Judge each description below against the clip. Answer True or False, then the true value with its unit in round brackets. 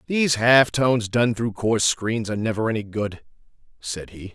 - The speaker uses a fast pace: False (180 wpm)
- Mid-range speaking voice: False (110 Hz)